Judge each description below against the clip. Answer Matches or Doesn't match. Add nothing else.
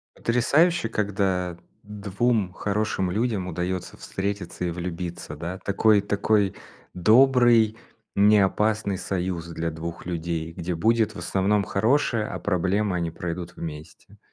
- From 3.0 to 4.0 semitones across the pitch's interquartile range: Matches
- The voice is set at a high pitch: Doesn't match